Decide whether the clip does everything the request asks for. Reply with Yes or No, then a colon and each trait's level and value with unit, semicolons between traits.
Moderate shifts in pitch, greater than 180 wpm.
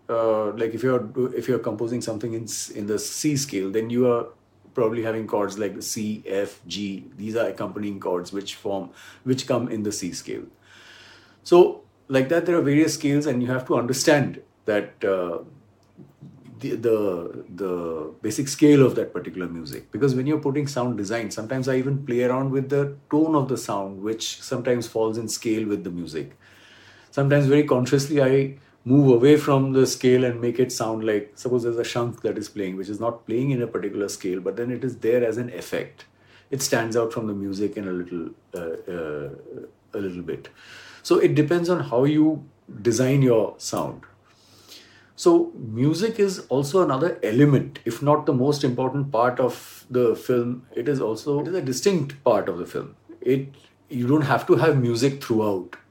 Yes: average, 4.3 semitones; average, 195 wpm